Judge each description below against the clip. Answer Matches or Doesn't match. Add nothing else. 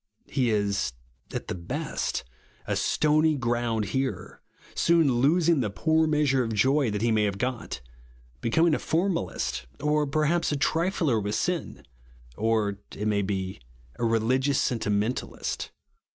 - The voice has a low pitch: Matches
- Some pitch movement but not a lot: Doesn't match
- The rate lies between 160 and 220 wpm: Doesn't match